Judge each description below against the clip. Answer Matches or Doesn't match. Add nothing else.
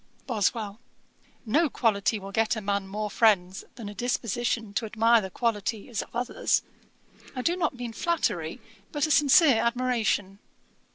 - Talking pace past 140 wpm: Matches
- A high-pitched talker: Matches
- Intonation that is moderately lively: Matches